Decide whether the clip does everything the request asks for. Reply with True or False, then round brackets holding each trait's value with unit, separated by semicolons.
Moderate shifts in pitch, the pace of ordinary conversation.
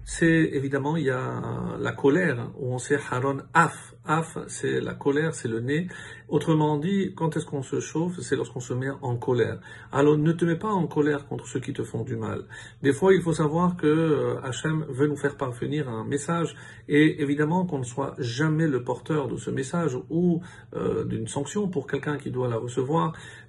True (3.4 semitones; 205 wpm)